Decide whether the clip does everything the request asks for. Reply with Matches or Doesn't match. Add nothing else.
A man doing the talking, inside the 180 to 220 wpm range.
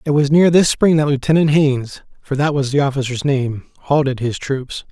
Matches